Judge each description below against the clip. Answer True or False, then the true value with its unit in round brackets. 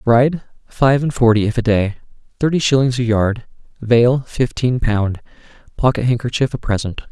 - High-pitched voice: False (120 Hz)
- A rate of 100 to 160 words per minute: True (150 wpm)